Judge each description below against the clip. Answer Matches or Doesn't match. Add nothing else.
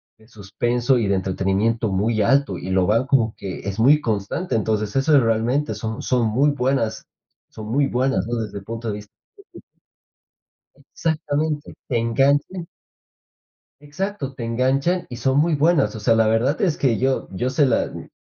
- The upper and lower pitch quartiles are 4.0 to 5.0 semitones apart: Matches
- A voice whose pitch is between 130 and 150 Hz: Doesn't match